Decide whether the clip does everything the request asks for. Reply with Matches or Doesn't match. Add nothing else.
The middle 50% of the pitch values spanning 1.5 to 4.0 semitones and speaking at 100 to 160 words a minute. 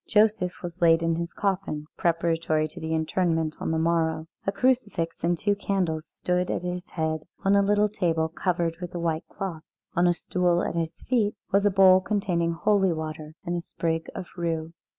Doesn't match